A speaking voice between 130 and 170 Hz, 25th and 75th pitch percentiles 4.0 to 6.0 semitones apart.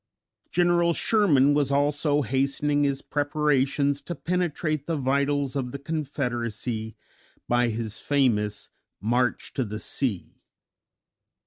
No: medium, 140 Hz; average, 3.2 semitones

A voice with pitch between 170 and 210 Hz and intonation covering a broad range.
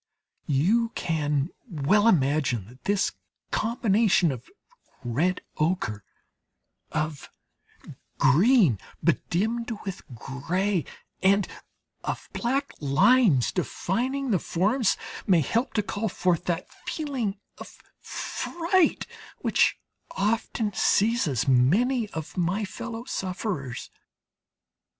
Yes: high, 190 Hz; wide, 7.1 semitones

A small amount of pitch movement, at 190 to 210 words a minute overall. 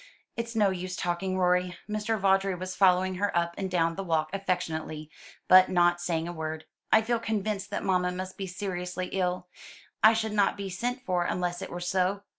Yes: narrow, 2.0 semitones; average, 195 wpm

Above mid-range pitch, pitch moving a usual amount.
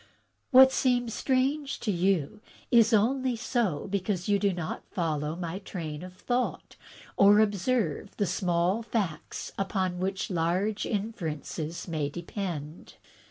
Yes: high, 195 Hz; average, 4.6 semitones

